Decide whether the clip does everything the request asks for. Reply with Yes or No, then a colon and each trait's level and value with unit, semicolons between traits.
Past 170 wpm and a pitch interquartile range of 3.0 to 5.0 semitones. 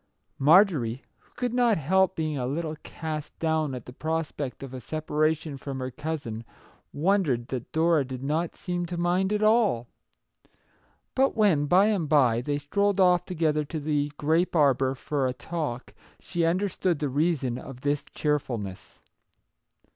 No: average, 160 wpm; average, 4.4 semitones